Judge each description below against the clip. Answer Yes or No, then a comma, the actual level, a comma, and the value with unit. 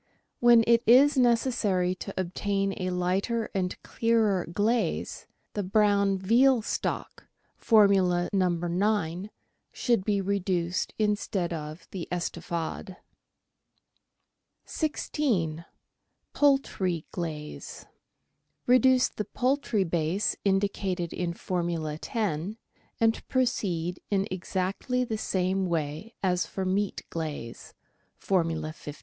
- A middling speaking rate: No, slow, 105 wpm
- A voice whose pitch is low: No, high, 190 Hz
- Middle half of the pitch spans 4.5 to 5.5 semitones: No, average, 4.1 semitones